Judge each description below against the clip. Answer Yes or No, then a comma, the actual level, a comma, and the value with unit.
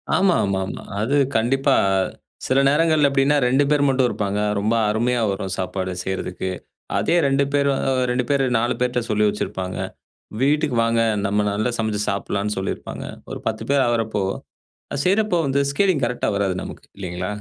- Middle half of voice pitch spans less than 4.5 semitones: No, wide, 5.5 semitones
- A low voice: Yes, low, 120 Hz